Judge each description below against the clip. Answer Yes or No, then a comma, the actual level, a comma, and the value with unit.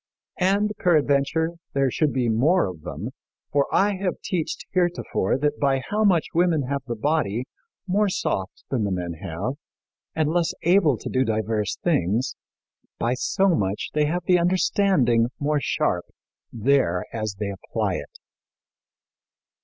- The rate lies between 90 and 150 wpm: Yes, average, 145 wpm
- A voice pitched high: No, medium, 140 Hz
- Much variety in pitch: Yes, wide, 7.5 semitones